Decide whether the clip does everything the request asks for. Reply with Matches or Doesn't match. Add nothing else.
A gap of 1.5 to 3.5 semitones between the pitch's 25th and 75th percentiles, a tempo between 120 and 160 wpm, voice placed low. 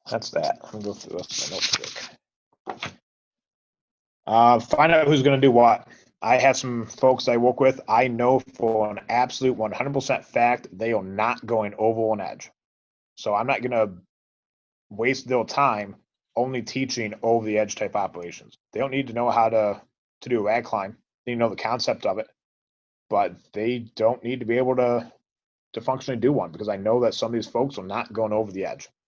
Doesn't match